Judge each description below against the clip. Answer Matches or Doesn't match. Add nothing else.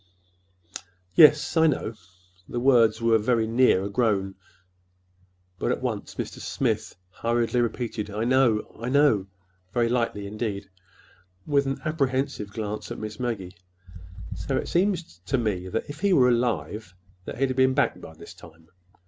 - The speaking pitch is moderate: Doesn't match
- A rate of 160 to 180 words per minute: Doesn't match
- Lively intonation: Doesn't match